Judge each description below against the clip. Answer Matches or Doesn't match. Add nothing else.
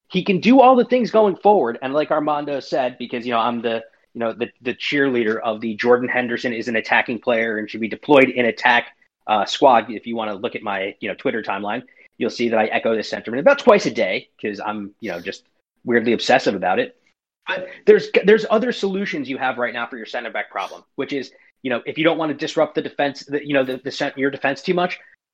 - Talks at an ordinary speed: Doesn't match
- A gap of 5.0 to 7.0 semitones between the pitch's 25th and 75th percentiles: Matches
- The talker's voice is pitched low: Matches